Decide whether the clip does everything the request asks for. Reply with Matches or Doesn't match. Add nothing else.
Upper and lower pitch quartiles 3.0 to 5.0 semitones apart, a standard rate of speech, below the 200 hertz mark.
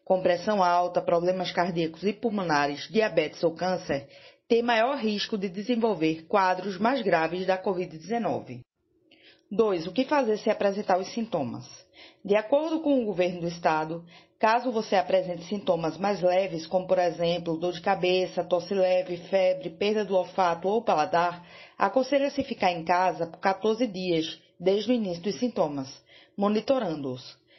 Matches